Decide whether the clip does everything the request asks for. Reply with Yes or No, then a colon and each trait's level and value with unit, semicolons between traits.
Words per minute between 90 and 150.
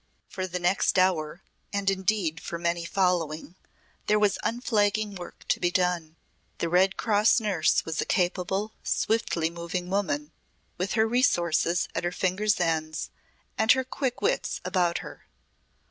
Yes: average, 145 wpm